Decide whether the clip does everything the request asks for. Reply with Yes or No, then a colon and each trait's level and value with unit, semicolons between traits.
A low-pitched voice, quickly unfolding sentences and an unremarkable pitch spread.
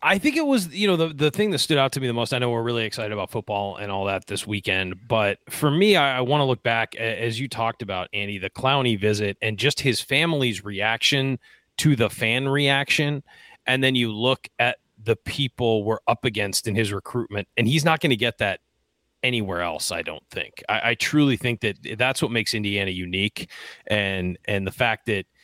Yes: low, 115 Hz; fast, 220 wpm; average, 4.5 semitones